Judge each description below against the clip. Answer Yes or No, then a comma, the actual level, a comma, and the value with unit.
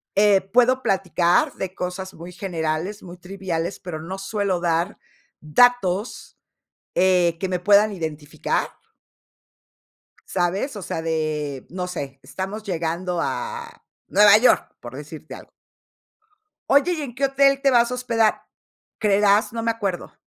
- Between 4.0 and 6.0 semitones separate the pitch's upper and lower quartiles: Yes, average, 4.5 semitones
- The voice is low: No, high, 190 Hz